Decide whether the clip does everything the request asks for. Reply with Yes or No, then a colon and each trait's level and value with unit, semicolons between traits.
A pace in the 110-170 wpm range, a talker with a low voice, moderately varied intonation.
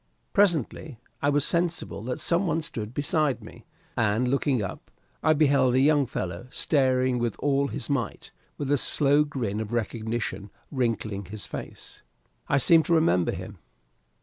Yes: average, 155 wpm; low, 130 Hz; average, 4.7 semitones